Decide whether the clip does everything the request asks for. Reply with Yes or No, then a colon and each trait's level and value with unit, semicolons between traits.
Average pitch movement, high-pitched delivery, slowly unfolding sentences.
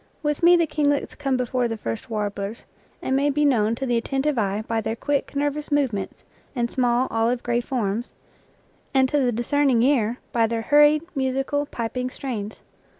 No: average, 4.0 semitones; very high, 250 Hz; average, 175 wpm